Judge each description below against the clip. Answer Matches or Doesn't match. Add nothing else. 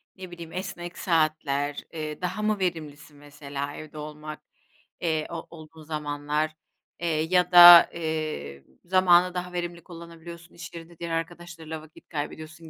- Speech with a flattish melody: Matches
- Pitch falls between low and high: Matches